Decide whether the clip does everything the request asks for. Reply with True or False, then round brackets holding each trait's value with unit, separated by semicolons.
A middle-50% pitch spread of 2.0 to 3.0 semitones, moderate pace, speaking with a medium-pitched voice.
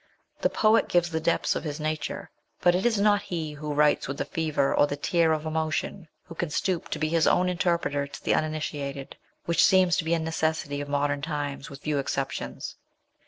False (2.7 semitones; 210 wpm; 155 Hz)